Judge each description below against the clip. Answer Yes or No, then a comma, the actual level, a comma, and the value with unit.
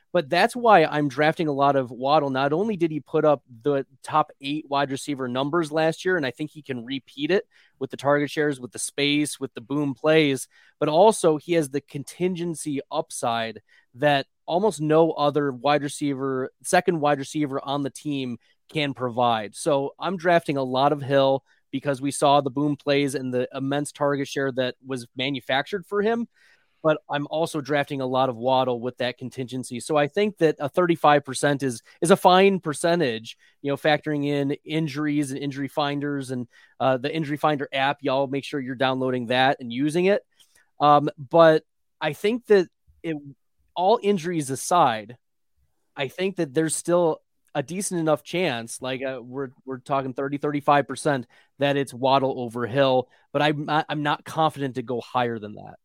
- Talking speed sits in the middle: Yes, average, 185 wpm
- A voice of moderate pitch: Yes, medium, 145 Hz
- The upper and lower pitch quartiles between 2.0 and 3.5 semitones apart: Yes, average, 2.8 semitones